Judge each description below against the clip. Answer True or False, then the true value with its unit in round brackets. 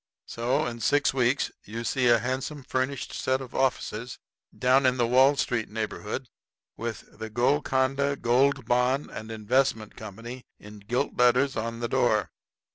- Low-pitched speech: True (125 Hz)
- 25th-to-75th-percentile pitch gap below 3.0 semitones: True (2.5 semitones)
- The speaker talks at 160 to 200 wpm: False (150 wpm)